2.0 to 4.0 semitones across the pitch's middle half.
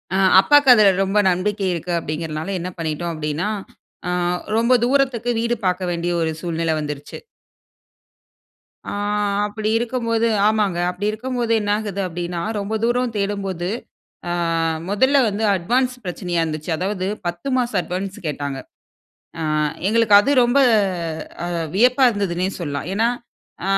No: average, 5.0 semitones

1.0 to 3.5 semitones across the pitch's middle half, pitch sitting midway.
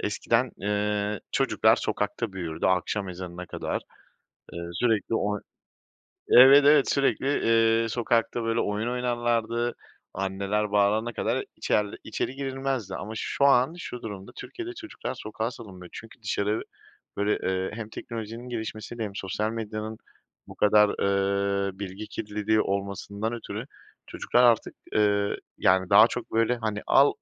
No: average, 2.8 semitones; low, 110 Hz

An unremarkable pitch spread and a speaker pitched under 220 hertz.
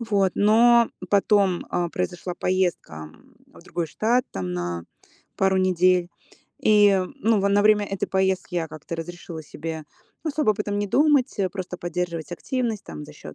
Yes: average, 3.4 semitones; high, 190 Hz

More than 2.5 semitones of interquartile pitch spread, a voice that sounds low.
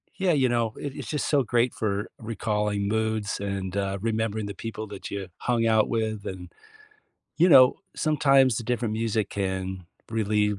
Yes: average, 2.9 semitones; low, 110 Hz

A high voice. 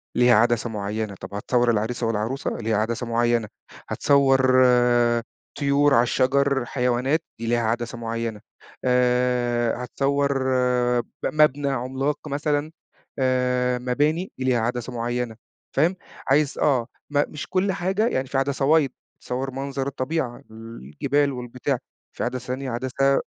No: low, 125 Hz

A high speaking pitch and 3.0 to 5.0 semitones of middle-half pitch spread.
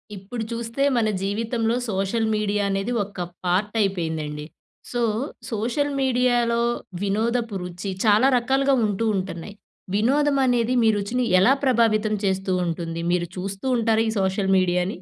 Yes: high, 215 Hz; average, 3.6 semitones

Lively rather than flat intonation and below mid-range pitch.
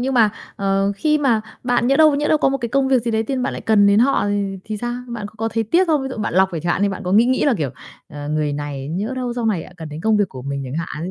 No: wide, 6.2 semitones; high, 215 Hz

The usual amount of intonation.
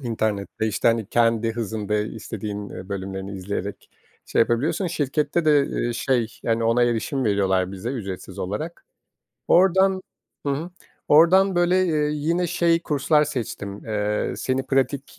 No: wide, 6.5 semitones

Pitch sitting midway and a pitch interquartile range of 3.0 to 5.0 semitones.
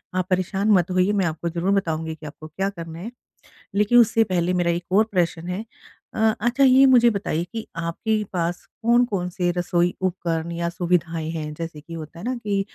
Yes: medium, 180 Hz; average, 3.4 semitones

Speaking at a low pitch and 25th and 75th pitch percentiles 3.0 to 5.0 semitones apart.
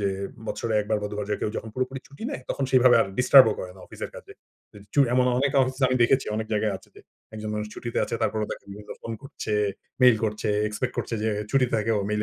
Yes: low, 115 Hz; average, 3.3 semitones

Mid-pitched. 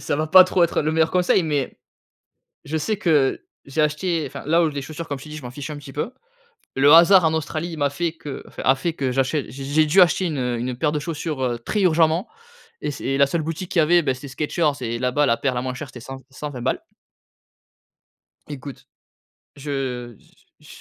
Yes: medium, 150 Hz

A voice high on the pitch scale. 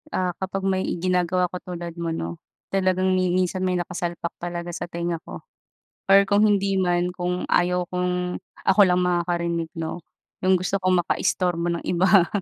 No: medium, 180 Hz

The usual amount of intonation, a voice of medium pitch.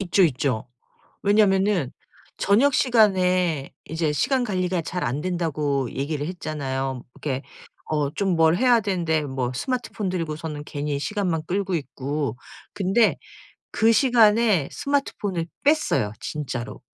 No: wide, 5.8 semitones; medium, 170 Hz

